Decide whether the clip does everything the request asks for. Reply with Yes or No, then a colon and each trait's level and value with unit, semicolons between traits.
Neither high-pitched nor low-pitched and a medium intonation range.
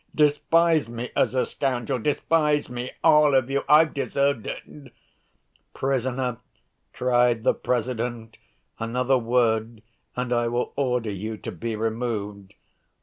No: low, 125 Hz; average, 3.2 semitones